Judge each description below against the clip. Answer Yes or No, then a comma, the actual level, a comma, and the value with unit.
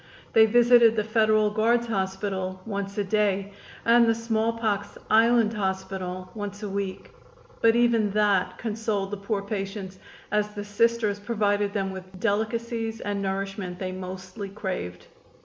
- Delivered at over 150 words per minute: No, average, 140 wpm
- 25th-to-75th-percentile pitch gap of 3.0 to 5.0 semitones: No, narrow, 2.5 semitones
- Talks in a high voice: Yes, high, 205 Hz